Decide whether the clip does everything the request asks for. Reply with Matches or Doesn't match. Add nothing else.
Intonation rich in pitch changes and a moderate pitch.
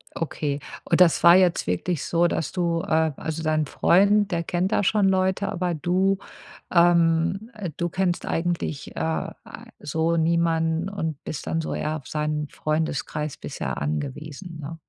Doesn't match